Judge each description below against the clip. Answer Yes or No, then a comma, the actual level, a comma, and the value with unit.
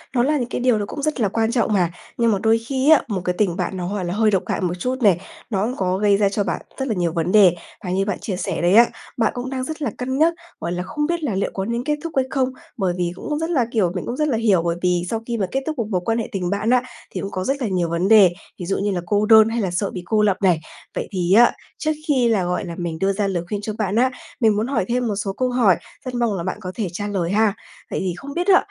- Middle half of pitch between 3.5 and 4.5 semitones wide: No, average, 4.9 semitones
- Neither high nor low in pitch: No, high, 210 Hz